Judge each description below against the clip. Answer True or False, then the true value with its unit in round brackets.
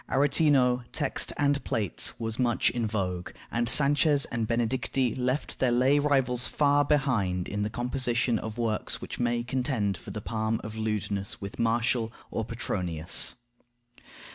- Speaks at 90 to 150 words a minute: True (145 wpm)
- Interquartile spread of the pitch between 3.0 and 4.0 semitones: True (3.5 semitones)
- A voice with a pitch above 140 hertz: False (120 Hz)